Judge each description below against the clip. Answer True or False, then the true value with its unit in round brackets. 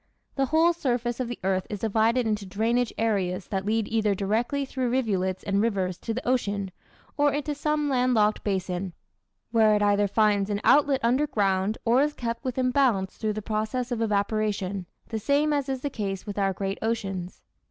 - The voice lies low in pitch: False (220 Hz)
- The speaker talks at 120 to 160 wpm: False (190 wpm)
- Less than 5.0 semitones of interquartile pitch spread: True (4.1 semitones)